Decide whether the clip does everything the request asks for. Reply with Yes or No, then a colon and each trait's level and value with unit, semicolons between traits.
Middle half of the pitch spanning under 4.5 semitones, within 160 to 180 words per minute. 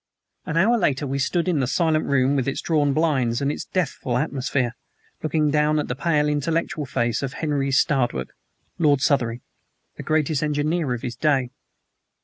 Yes: average, 2.9 semitones; average, 170 wpm